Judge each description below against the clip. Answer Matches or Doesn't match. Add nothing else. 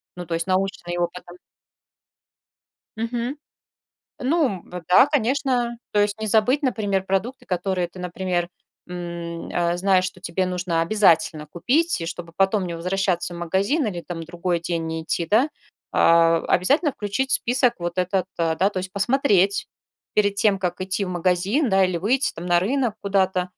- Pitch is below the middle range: Doesn't match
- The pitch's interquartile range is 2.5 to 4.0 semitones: Matches